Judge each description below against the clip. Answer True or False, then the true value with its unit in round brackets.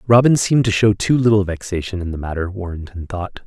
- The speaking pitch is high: False (100 Hz)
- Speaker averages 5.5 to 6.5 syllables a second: True (6.1 syllables/s)